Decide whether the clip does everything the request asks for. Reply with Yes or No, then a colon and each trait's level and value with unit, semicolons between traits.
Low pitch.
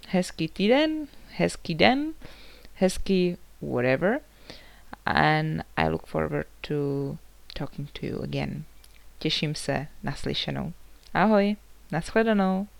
No: medium, 155 Hz